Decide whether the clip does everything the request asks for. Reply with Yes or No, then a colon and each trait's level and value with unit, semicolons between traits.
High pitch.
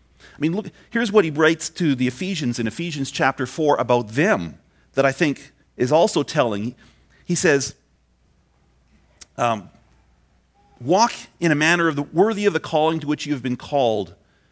No: low, 135 Hz